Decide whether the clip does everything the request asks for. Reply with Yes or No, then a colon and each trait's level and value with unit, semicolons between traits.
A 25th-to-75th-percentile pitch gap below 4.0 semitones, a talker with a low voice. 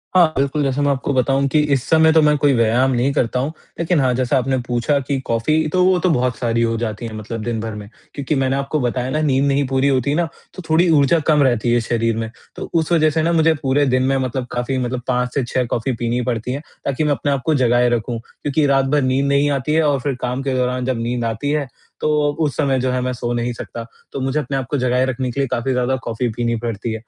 Yes: average, 2.8 semitones; low, 130 Hz